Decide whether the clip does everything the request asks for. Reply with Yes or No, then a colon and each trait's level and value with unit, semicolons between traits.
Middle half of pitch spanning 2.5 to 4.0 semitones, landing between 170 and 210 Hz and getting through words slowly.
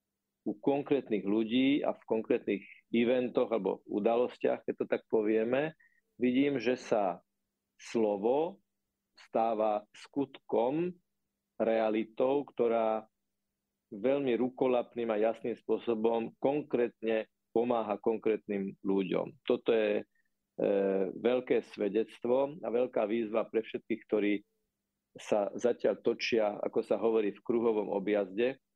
No: average, 2.8 semitones; low, 115 Hz; slow, 105 wpm